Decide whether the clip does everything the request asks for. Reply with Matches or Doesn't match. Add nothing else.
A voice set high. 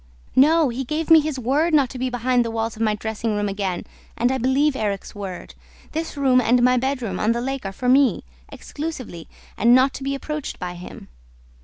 Matches